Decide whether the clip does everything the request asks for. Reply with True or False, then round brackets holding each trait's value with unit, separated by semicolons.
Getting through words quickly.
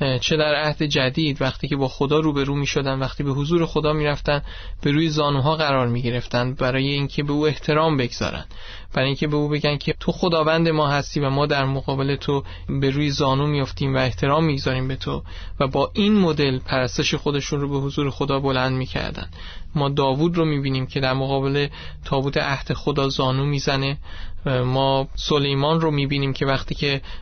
True (195 wpm)